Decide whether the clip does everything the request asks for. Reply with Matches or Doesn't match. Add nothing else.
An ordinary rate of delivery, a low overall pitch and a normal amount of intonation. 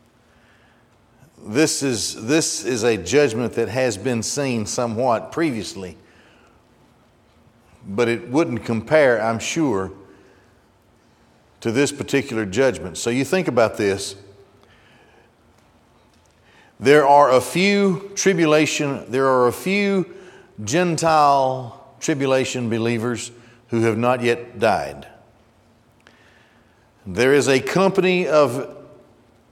Doesn't match